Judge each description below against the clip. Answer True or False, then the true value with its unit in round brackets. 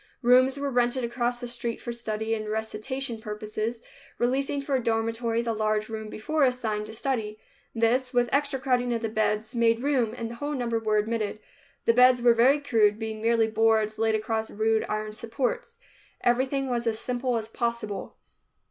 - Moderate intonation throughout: False (2.3 semitones)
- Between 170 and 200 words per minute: True (180 wpm)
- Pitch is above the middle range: True (230 Hz)